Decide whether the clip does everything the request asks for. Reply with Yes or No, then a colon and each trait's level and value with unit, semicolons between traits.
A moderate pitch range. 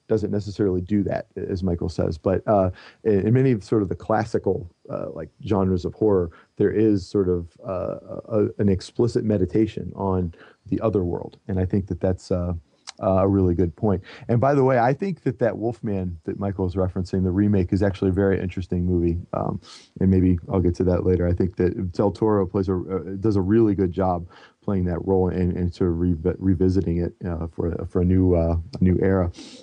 No: narrow, 2.3 semitones